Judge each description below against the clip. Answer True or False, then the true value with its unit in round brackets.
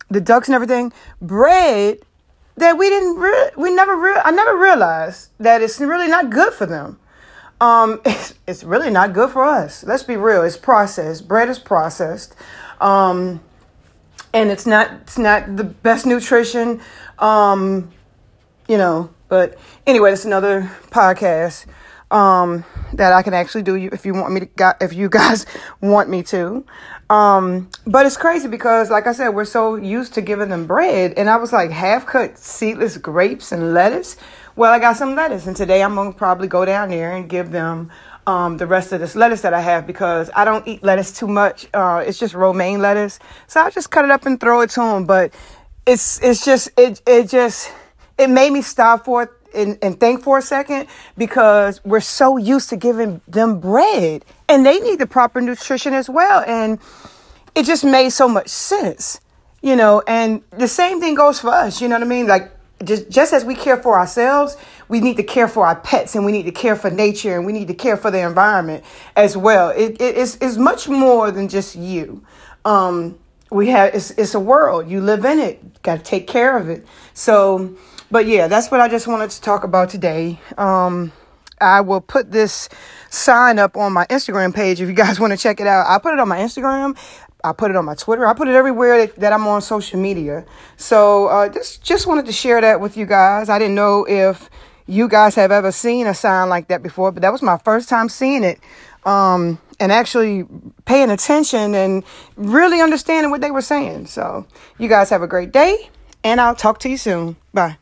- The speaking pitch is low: False (215 Hz)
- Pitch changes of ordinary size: True (4.6 semitones)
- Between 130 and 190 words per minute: False (205 wpm)